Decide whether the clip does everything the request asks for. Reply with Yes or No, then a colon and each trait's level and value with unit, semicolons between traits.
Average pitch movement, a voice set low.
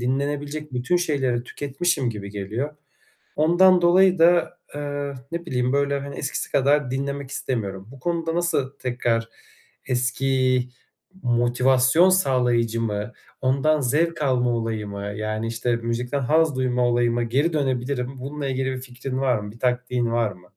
Yes: average, 3.2 semitones; low, 130 Hz